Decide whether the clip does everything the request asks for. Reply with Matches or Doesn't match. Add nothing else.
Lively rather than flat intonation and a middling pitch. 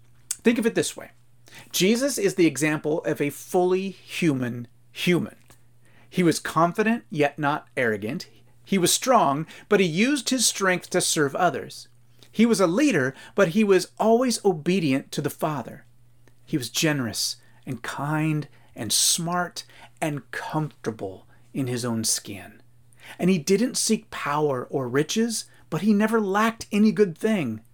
Matches